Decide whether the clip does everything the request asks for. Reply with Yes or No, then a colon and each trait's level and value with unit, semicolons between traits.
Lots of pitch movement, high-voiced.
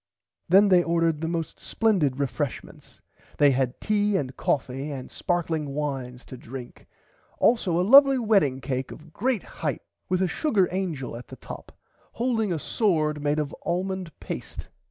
No: wide, 5.7 semitones; medium, 165 Hz